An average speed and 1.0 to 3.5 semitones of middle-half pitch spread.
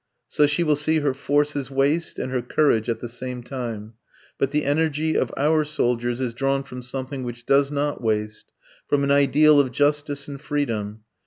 Yes: average, 185 wpm; average, 3.1 semitones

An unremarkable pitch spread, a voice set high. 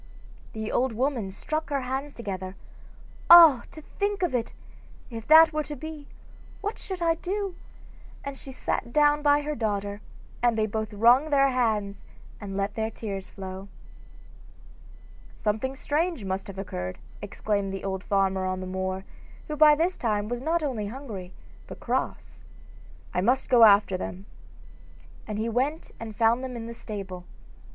No: wide, 6.5 semitones; high, 230 Hz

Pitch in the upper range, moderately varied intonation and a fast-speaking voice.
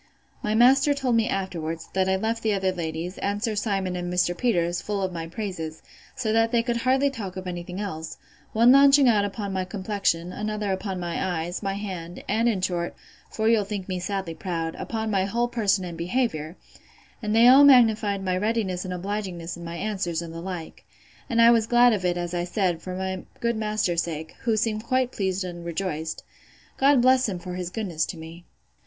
Yes: high, 195 Hz; average, 4.1 semitones; fast, 210 wpm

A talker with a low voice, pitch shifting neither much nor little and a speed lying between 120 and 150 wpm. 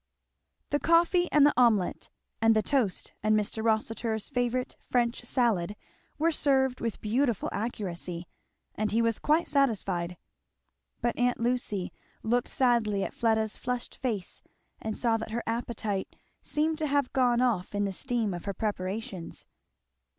No: high, 230 Hz; average, 3.2 semitones; average, 145 wpm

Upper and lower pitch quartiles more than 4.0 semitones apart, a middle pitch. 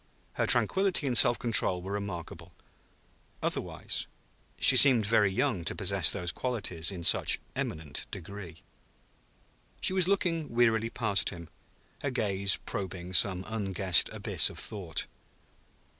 No: average, 5.1 semitones; low, 100 Hz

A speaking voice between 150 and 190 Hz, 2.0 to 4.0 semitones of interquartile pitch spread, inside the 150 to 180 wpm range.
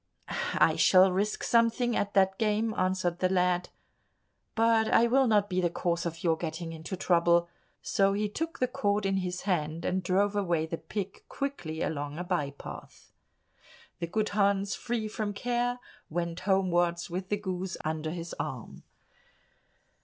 Yes: medium, 185 Hz; average, 3.4 semitones; average, 160 wpm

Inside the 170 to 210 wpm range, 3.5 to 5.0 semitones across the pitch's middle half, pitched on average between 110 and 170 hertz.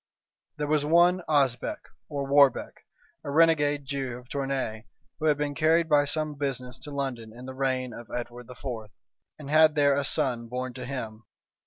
No: average, 175 wpm; average, 2.9 semitones; medium, 140 Hz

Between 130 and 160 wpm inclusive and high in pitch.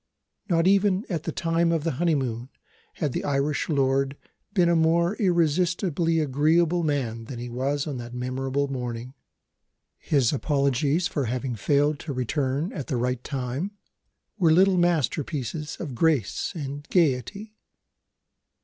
No: average, 140 wpm; medium, 145 Hz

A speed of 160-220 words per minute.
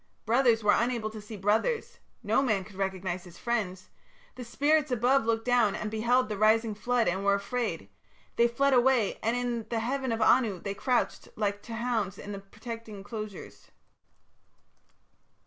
Yes: average, 165 wpm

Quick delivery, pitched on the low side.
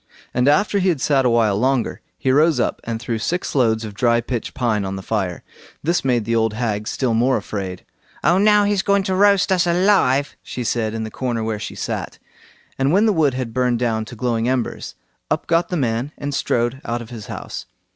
Yes: fast, 220 wpm; low, 125 Hz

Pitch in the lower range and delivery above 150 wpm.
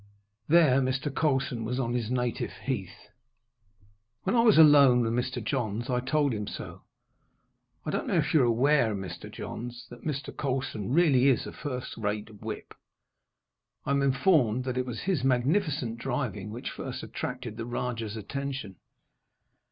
Yes: low, 125 Hz; average, 160 wpm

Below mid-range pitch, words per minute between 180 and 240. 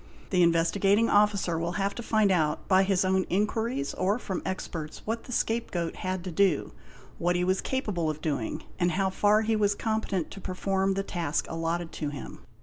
No: high, 190 Hz; average, 190 wpm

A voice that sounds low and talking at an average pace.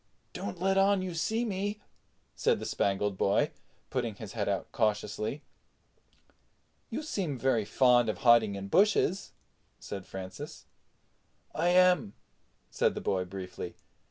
No: low, 120 Hz; slow, 130 wpm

